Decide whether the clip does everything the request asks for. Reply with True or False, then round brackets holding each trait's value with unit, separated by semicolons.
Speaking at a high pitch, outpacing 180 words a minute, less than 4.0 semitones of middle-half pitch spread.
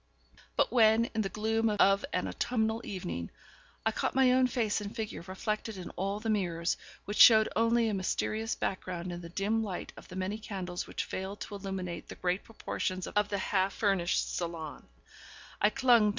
True (205 Hz; 190 wpm; 3.1 semitones)